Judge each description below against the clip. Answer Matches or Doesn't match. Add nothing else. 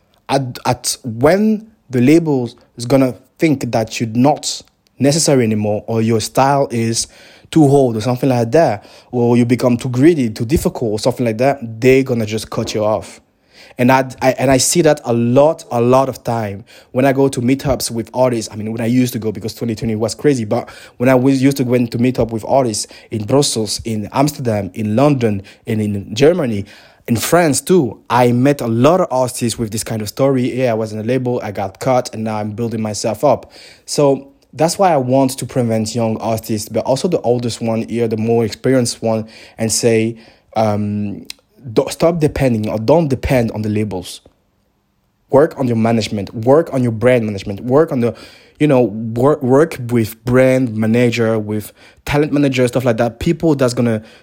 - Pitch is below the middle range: Matches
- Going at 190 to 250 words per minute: Matches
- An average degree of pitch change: Matches